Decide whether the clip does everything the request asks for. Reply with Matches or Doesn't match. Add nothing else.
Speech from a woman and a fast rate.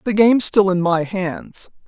Doesn't match